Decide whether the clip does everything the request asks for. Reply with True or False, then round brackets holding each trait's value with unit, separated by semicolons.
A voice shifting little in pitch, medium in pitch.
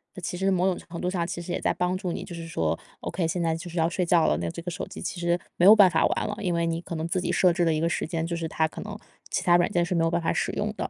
True (1.7 semitones; 175 Hz)